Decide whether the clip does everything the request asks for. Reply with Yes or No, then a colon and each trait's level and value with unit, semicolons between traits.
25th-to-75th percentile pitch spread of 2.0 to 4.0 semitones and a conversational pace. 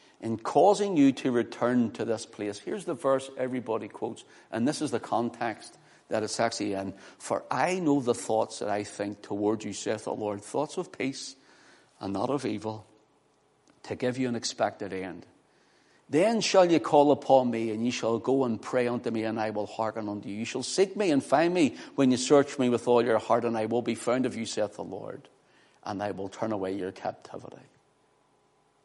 No: average, 3.7 semitones; fast, 210 wpm